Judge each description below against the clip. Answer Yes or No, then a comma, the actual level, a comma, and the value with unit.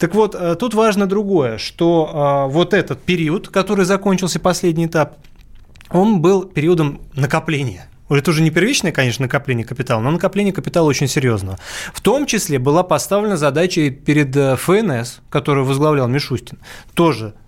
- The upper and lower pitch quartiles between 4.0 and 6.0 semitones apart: Yes, average, 5.1 semitones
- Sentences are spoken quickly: No, average, 140 wpm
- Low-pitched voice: No, medium, 155 Hz